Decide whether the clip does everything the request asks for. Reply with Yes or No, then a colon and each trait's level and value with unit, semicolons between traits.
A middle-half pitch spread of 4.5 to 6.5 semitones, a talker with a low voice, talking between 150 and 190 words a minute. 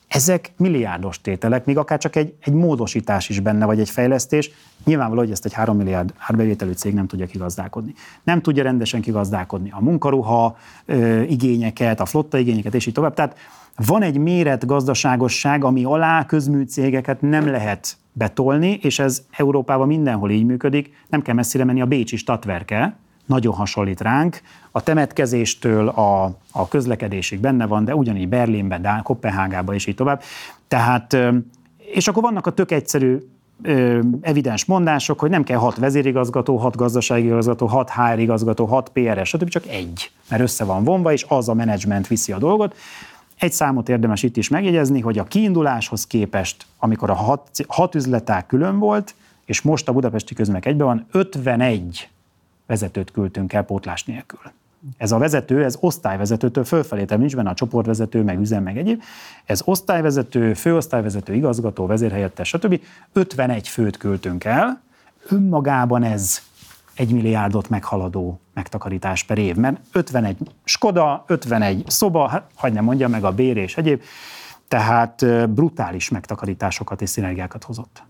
Yes: average, 5.2 semitones; low, 120 Hz; fast, 155 wpm